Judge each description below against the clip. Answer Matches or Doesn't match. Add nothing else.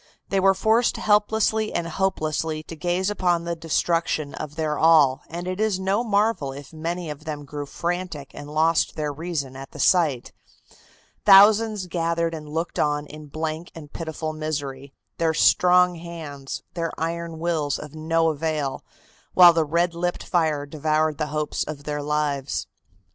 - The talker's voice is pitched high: Doesn't match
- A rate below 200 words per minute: Matches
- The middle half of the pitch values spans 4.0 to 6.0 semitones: Doesn't match